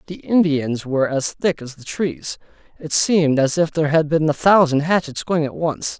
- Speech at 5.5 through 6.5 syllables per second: No, 5.0 syllables/s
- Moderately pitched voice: Yes, medium, 155 Hz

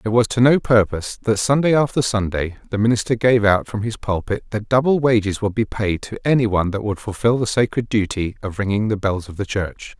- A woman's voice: No, male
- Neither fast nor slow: No, fast, 220 wpm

